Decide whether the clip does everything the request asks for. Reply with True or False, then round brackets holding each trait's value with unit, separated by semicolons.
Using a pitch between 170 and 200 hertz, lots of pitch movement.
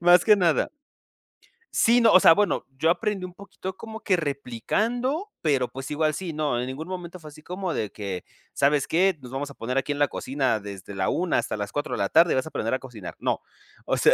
False (155 Hz; 6.0 semitones)